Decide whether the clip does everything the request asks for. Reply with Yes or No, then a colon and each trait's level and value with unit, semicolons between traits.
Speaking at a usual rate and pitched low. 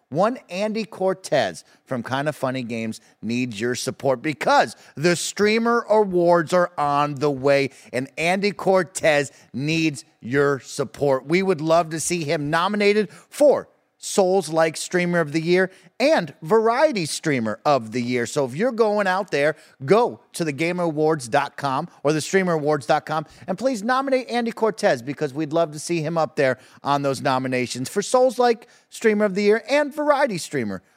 No: average, 155 wpm; medium, 165 Hz